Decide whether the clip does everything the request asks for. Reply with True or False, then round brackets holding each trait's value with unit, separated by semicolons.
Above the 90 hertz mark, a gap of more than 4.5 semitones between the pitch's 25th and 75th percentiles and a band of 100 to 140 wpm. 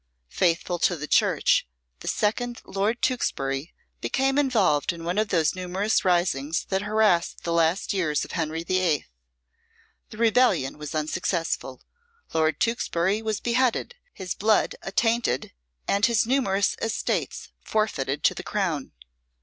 True (185 Hz; 5.2 semitones; 135 wpm)